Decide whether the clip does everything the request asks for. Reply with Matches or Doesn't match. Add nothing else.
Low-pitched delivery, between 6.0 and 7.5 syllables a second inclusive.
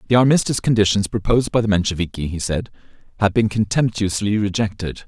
Matches